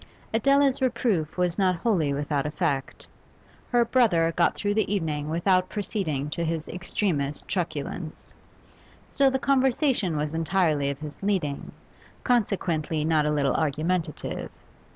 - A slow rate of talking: Yes, slow, 130 wpm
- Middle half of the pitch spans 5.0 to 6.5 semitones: Yes, wide, 5.4 semitones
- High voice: No, medium, 170 Hz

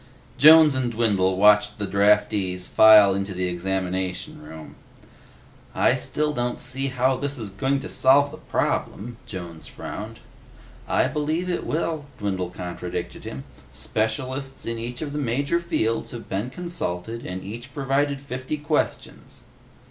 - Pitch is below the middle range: Yes, low, 115 Hz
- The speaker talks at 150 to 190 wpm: No, average, 140 wpm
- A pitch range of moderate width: No, wide, 6.5 semitones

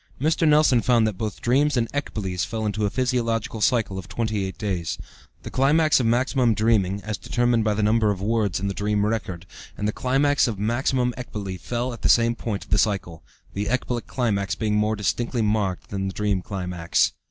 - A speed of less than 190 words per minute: No, average, 200 wpm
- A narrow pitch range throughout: No, average, 3.3 semitones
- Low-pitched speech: Yes, low, 110 Hz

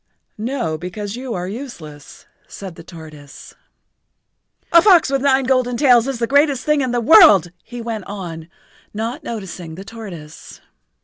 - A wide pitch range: Yes, wide, 7.0 semitones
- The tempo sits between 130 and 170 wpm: Yes, average, 150 wpm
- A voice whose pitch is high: Yes, high, 225 Hz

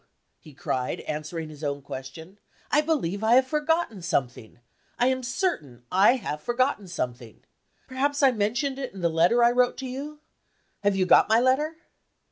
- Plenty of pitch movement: Yes, wide, 8.5 semitones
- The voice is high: Yes, high, 215 Hz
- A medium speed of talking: Yes, average, 170 wpm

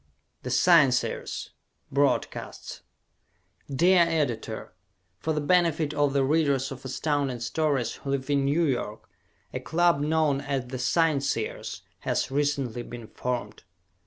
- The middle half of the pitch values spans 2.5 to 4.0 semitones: Yes, average, 3.4 semitones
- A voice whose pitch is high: No, medium, 140 Hz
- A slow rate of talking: Yes, slow, 125 wpm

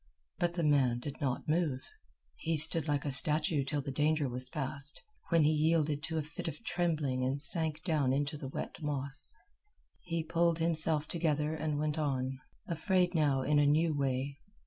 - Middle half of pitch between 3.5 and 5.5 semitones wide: No, narrow, 2.6 semitones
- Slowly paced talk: No, average, 180 wpm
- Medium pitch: Yes, medium, 150 Hz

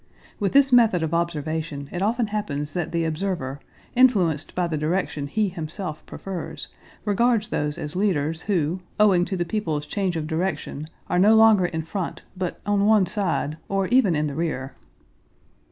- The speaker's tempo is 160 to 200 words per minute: Yes, average, 170 wpm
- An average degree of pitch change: Yes, average, 4.7 semitones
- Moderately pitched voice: Yes, medium, 175 Hz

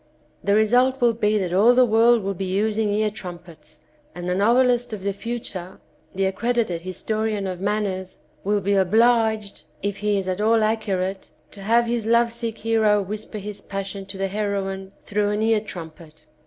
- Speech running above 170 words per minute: Yes, average, 180 wpm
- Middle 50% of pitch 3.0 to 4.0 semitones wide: No, narrow, 2.6 semitones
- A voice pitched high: Yes, high, 210 Hz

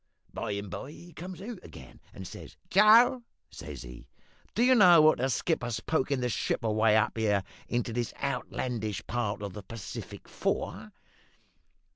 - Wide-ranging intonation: Yes, wide, 8.1 semitones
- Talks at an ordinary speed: Yes, average, 165 wpm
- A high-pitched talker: No, low, 120 Hz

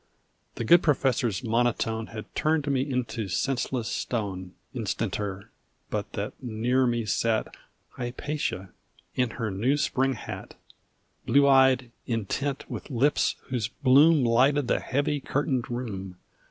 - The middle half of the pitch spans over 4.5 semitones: No, average, 3.4 semitones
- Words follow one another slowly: Yes, slow, 125 wpm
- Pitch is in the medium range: No, low, 125 Hz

